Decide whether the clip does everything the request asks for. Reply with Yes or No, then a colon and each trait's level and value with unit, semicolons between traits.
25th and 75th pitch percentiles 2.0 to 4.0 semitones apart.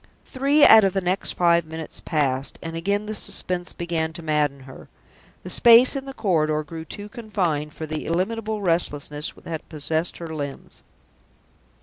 No: average, 4.8 semitones